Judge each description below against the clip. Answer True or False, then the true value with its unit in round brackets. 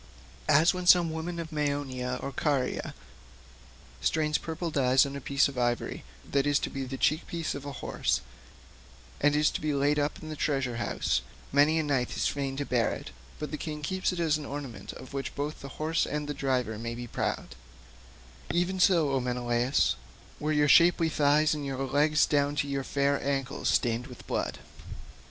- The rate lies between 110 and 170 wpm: False (185 wpm)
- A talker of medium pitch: True (145 Hz)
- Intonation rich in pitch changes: False (2.7 semitones)